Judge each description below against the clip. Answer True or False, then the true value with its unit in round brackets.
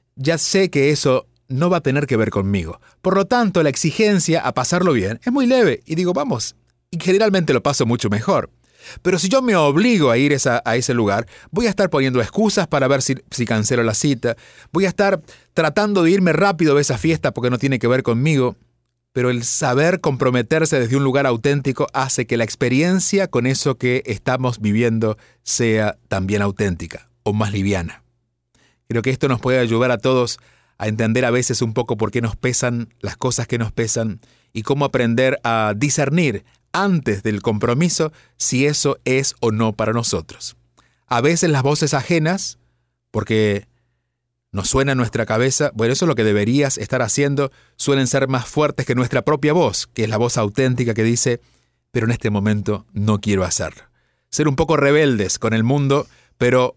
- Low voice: True (125 Hz)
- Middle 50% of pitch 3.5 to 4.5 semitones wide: True (4.2 semitones)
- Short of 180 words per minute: False (190 wpm)